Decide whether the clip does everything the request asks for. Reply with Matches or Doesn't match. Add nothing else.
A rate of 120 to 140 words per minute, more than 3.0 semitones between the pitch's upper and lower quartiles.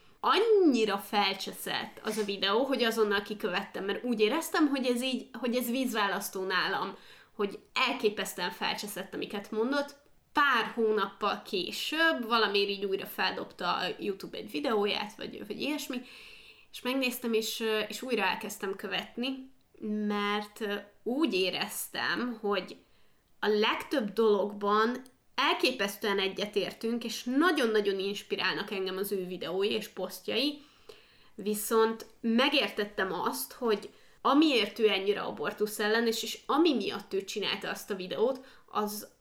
Matches